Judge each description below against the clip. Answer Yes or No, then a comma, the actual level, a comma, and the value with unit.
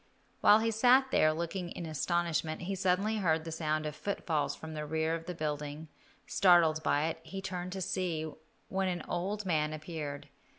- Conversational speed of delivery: Yes, average, 180 wpm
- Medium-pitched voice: Yes, medium, 165 Hz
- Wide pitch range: No, average, 3.3 semitones